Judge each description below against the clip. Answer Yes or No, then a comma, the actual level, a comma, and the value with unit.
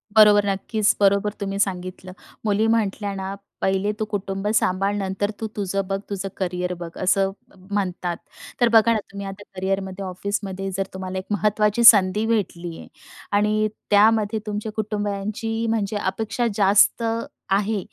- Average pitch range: No, narrow, 1.7 semitones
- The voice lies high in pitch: Yes, high, 200 Hz